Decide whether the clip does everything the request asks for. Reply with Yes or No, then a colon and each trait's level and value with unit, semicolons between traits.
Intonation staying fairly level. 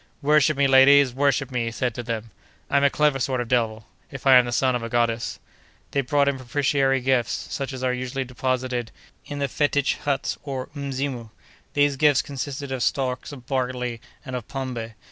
Yes: narrow, 2.3 semitones